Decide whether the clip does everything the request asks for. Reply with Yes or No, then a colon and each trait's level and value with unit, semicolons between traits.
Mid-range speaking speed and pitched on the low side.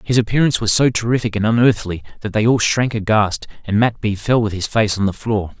No: fast, 235 wpm; low, 110 Hz